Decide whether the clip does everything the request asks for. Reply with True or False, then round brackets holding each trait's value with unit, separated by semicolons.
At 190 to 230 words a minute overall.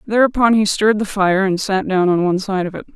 False (265 wpm)